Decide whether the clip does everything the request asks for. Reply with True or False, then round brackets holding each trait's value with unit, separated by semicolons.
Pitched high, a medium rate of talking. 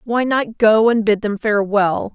True (215 Hz; 195 wpm)